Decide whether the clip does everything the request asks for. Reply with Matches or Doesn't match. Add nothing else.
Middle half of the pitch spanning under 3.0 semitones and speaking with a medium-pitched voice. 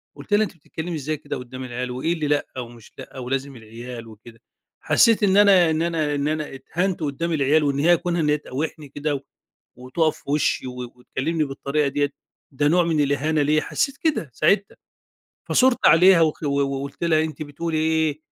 Doesn't match